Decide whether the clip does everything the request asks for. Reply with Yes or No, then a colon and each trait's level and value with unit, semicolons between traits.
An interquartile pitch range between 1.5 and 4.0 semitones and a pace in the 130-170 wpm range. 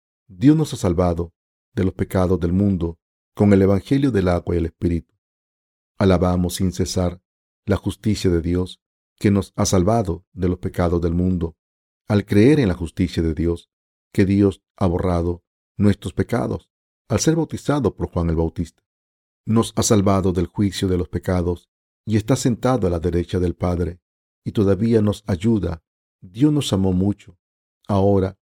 Yes: average, 2.8 semitones; average, 165 wpm